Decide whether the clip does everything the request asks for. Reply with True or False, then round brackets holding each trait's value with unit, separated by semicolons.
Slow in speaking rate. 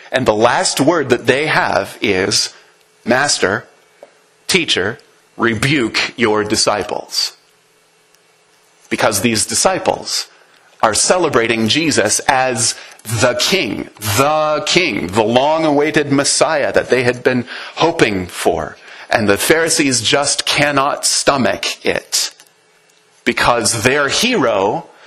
True (105 wpm)